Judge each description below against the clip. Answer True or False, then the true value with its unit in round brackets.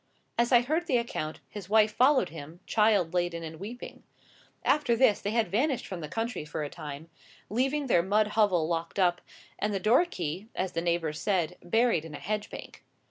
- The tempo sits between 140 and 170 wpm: False (195 wpm)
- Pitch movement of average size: False (5.7 semitones)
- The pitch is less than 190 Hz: False (205 Hz)